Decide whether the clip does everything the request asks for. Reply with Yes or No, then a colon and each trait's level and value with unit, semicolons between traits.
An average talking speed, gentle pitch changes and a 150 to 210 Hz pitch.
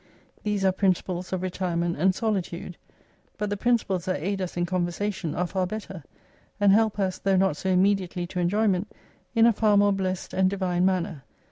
Yes: average, 180 wpm; narrow, 2.1 semitones; high, 190 Hz